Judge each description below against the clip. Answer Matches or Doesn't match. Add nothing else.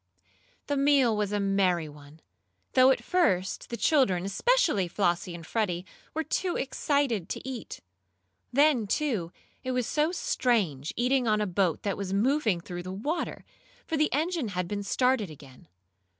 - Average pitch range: Doesn't match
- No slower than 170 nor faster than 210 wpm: Doesn't match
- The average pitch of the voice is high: Matches